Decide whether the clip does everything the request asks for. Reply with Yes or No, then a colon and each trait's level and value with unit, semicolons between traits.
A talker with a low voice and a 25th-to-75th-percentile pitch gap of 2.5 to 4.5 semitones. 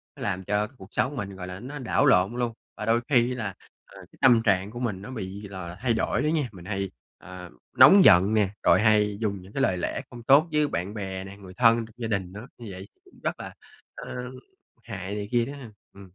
Yes: low, 105 Hz; average, 4.1 semitones